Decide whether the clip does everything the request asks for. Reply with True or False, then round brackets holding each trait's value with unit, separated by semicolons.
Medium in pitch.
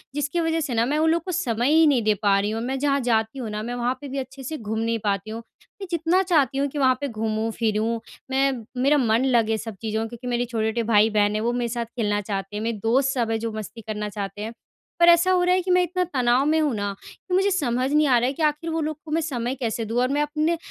False (245 Hz)